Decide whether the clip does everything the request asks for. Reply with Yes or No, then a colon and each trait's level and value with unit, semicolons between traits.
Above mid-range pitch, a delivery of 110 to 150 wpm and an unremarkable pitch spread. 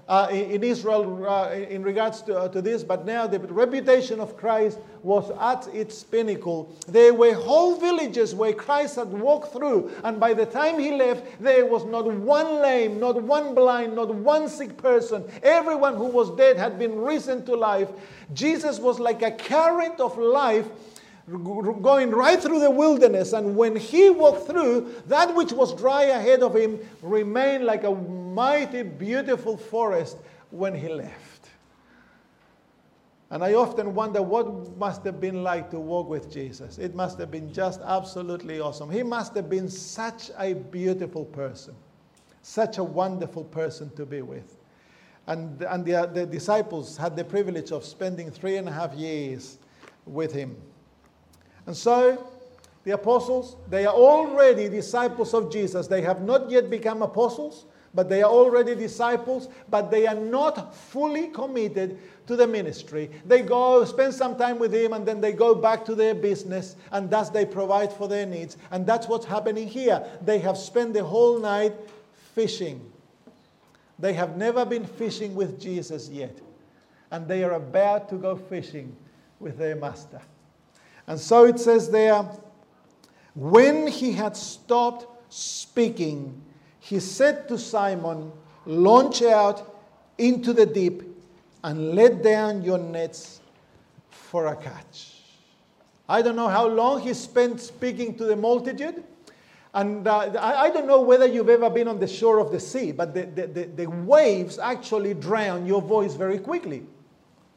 No: high, 215 Hz; average, 160 wpm; average, 4.7 semitones